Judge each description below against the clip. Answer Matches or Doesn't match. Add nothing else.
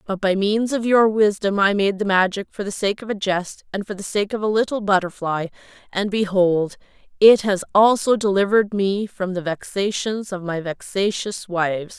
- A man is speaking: Doesn't match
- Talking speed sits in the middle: Matches